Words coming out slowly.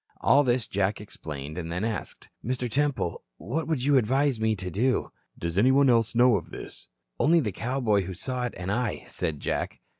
No: average, 190 wpm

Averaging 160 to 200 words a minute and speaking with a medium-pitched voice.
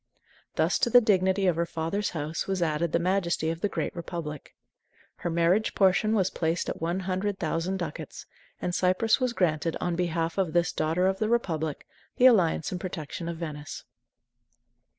Yes: average, 175 wpm; medium, 175 Hz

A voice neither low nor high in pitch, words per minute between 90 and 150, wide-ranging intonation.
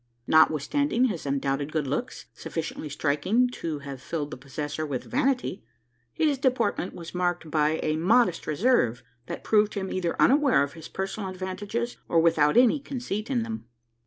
No: medium, 180 Hz; average, 160 wpm; wide, 7.8 semitones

